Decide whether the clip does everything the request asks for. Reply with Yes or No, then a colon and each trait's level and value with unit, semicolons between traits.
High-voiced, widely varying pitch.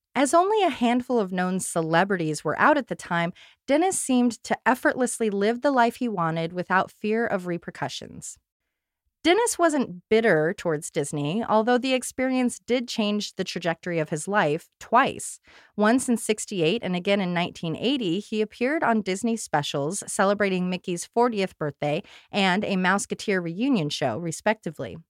Yes: high, 205 Hz; wide, 5.7 semitones